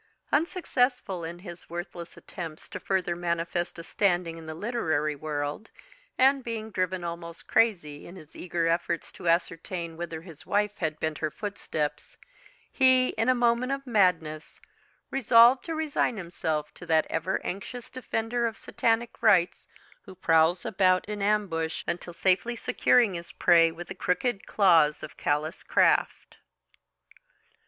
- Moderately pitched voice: Yes, medium, 180 Hz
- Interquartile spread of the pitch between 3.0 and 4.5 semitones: No, wide, 5.4 semitones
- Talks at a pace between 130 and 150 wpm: Yes, average, 145 wpm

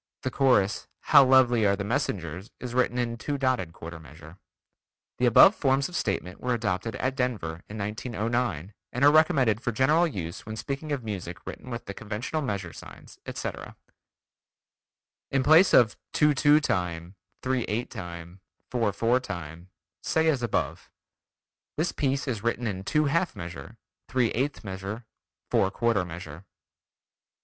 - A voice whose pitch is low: Yes, low, 115 Hz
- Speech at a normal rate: Yes, average, 155 wpm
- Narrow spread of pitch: No, wide, 5.6 semitones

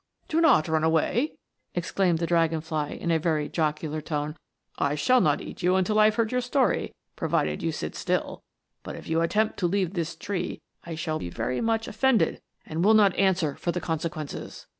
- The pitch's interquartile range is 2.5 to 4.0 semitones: No, average, 5.1 semitones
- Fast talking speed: Yes, fast, 210 wpm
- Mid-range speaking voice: Yes, medium, 170 Hz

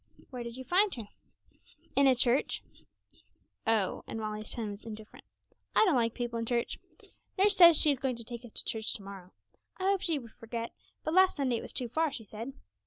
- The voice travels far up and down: No, average, 4.1 semitones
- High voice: Yes, high, 240 Hz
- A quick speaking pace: Yes, fast, 210 wpm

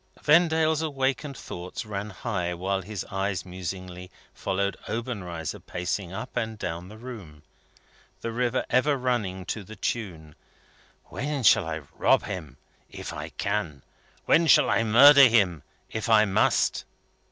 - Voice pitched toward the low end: Yes, low, 105 Hz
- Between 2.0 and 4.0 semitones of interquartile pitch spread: No, wide, 5.5 semitones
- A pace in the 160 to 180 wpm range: No, average, 140 wpm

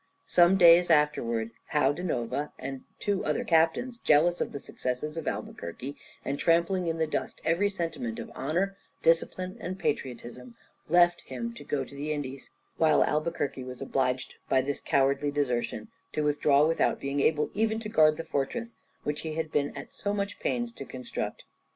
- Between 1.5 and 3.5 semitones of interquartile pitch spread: No, average, 4.1 semitones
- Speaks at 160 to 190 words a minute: Yes, average, 175 wpm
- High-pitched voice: No, medium, 150 Hz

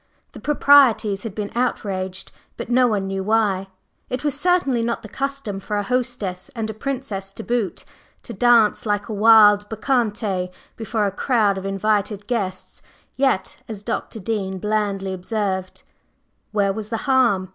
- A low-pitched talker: No, high, 215 Hz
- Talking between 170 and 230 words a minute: No, average, 160 wpm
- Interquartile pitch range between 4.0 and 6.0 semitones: No, average, 3.5 semitones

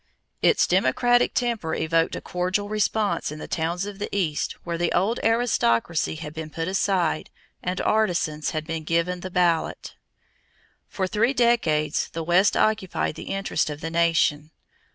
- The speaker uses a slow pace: No, average, 155 wpm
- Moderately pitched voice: Yes, medium, 175 Hz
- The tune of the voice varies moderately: Yes, average, 4.1 semitones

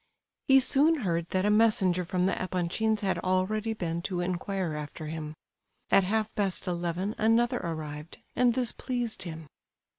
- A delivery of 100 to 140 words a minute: No, average, 155 wpm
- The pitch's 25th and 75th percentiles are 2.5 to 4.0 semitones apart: No, average, 4.4 semitones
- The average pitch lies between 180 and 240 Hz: Yes, medium, 185 Hz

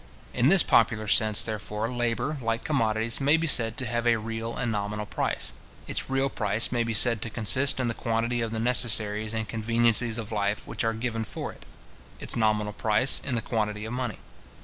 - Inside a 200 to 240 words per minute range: Yes, fast, 205 wpm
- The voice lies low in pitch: Yes, low, 115 Hz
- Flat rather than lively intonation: Yes, narrow, 1.9 semitones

